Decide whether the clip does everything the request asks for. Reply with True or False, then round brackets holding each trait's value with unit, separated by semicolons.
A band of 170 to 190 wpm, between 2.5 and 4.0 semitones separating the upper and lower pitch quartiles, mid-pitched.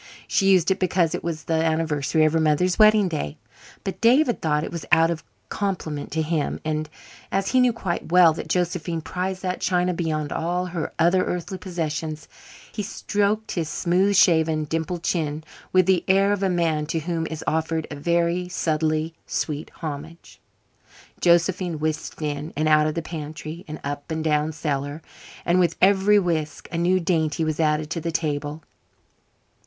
True (175 wpm; 2.8 semitones; 165 Hz)